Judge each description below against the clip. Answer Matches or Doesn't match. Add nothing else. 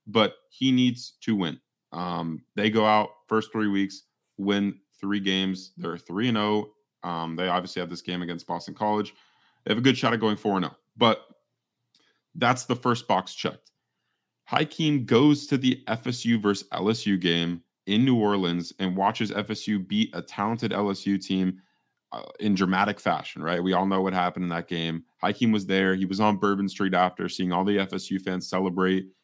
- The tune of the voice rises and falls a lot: Doesn't match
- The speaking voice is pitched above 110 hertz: Doesn't match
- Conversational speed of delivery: Matches